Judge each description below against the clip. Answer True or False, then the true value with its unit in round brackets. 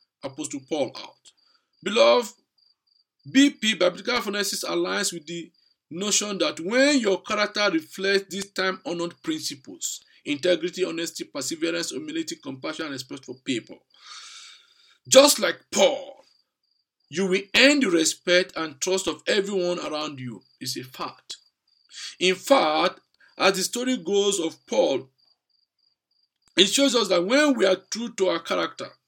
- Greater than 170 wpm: False (135 wpm)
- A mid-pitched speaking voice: False (195 Hz)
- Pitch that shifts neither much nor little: False (7.0 semitones)